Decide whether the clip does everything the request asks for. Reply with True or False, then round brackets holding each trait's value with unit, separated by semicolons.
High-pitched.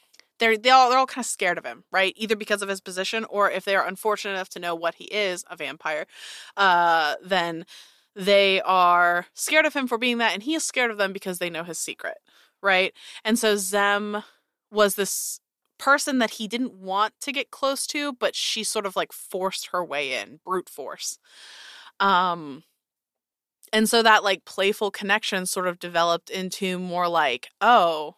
True (195 Hz)